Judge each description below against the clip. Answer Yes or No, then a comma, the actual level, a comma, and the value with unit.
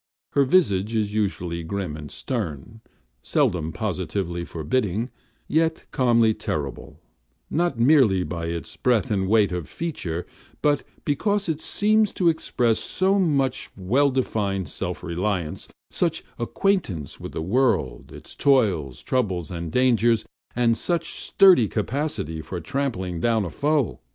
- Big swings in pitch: Yes, wide, 7.8 semitones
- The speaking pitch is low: Yes, low, 110 Hz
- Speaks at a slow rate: Yes, slow, 130 wpm